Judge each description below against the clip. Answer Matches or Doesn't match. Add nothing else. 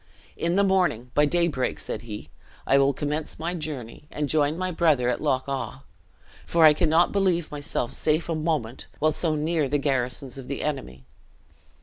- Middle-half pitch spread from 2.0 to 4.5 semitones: Matches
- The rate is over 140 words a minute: Matches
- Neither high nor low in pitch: Matches